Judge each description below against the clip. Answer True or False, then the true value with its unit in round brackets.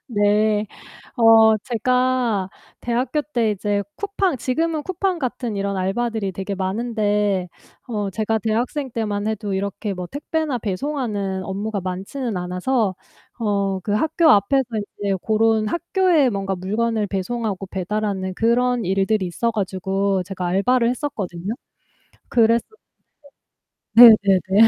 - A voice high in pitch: True (215 Hz)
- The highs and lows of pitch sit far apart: False (3.7 semitones)